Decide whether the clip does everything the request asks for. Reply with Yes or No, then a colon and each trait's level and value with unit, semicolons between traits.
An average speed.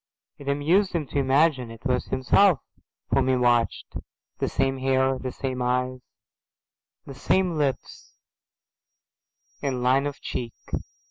No: slow, 130 wpm